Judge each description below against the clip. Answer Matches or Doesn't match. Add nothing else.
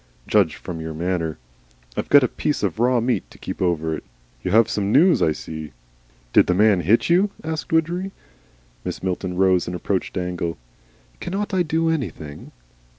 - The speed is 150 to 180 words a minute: Matches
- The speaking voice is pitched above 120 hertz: Doesn't match